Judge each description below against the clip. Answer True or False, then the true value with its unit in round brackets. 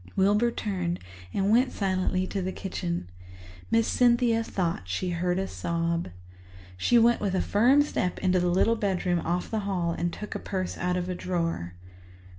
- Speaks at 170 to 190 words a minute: True (175 wpm)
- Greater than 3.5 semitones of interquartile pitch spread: False (3.2 semitones)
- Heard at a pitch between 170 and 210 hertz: True (185 Hz)